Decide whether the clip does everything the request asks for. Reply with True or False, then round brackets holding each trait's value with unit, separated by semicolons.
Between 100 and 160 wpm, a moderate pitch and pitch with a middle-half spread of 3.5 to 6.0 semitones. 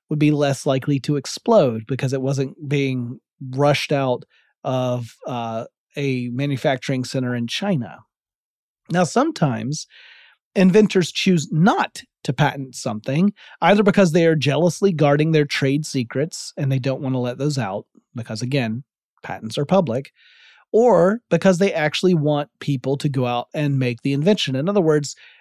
True (155 wpm; 145 Hz; 4.4 semitones)